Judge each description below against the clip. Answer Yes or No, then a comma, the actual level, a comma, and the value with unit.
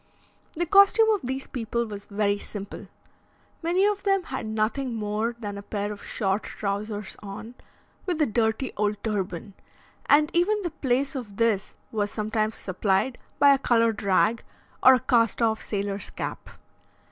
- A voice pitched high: Yes, high, 225 Hz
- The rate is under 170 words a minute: Yes, average, 160 wpm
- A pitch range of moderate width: Yes, average, 4.6 semitones